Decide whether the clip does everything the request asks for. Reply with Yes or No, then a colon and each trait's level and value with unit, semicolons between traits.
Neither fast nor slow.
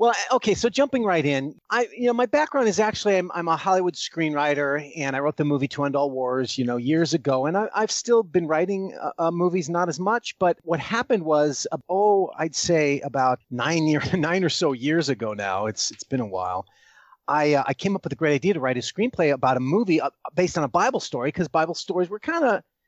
No: fast, 235 wpm